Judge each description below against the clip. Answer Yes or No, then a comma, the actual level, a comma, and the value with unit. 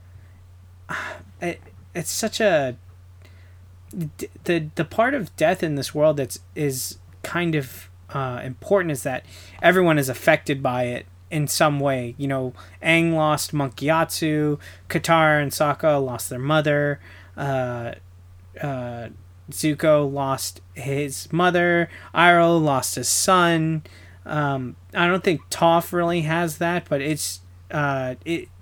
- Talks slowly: Yes, slow, 130 wpm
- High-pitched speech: No, medium, 140 Hz